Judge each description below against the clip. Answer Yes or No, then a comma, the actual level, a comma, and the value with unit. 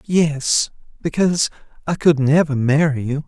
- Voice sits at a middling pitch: Yes, medium, 150 Hz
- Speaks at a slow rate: Yes, slow, 110 wpm